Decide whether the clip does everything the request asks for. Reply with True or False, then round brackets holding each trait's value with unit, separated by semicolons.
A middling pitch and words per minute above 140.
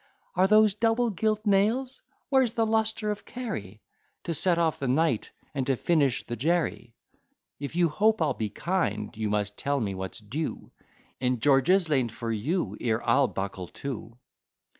True (150 Hz; 165 wpm)